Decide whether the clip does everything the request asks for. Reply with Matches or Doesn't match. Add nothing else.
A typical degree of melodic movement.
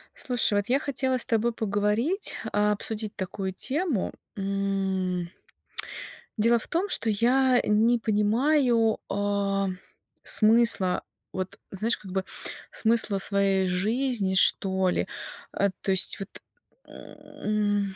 Matches